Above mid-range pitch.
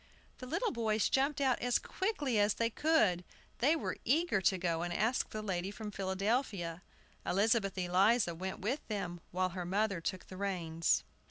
Yes: high, 200 Hz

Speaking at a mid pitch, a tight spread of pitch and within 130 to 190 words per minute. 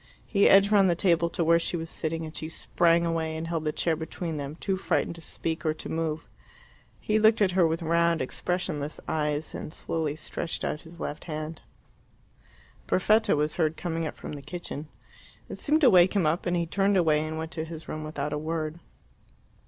No: medium, 165 Hz; narrow, 2.0 semitones; fast, 205 wpm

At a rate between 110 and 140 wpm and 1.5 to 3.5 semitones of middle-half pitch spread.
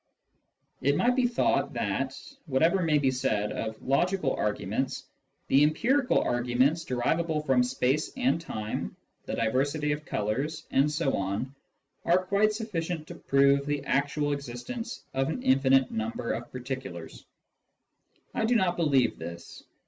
No: slow, 135 wpm; average, 4.7 semitones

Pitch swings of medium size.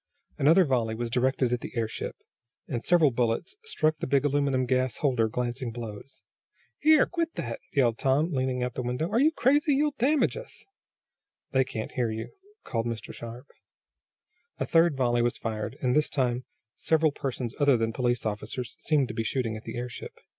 Yes: average, 4.1 semitones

